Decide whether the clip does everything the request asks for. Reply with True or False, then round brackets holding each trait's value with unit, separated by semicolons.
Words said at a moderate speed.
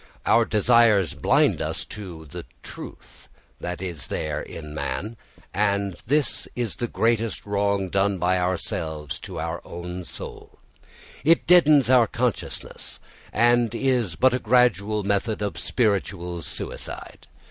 False (130 wpm)